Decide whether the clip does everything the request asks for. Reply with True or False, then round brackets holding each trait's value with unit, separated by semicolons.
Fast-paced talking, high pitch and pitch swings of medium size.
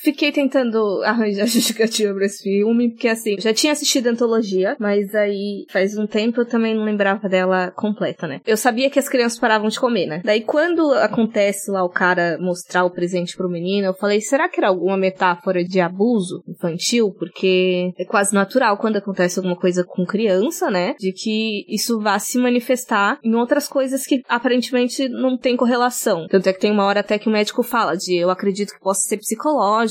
True (200 wpm; 210 Hz; 4.1 semitones)